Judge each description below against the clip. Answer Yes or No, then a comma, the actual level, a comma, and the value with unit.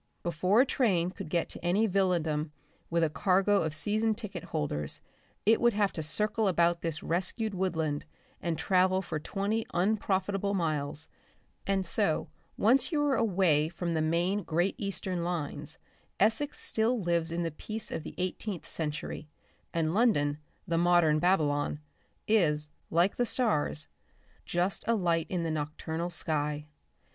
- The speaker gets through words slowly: No, average, 150 wpm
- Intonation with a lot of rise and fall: No, average, 4.1 semitones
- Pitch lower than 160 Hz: No, medium, 175 Hz